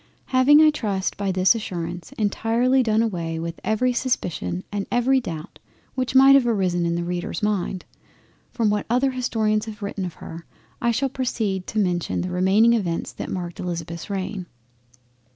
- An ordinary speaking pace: Yes, average, 165 wpm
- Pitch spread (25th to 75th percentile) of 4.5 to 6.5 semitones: Yes, average, 5.0 semitones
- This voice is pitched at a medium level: No, high, 205 Hz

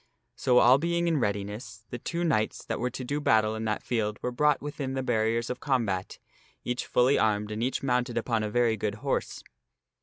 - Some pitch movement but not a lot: Yes, average, 3.4 semitones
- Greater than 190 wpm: Yes, fast, 205 wpm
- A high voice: No, low, 120 Hz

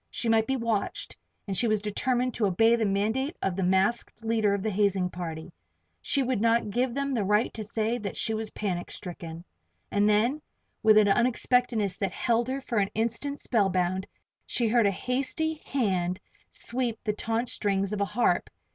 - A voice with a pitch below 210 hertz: No, high, 220 Hz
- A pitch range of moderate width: Yes, average, 3.4 semitones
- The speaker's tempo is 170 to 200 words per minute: Yes, average, 185 wpm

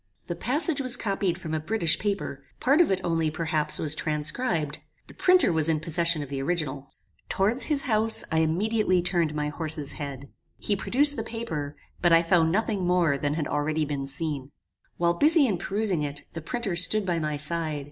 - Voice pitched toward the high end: No, medium, 170 Hz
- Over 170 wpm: Yes, average, 190 wpm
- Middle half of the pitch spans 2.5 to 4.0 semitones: No, wide, 5.4 semitones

